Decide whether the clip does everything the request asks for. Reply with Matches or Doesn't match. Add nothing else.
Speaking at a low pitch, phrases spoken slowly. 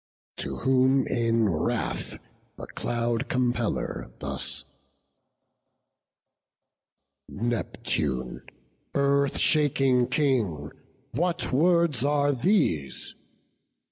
Matches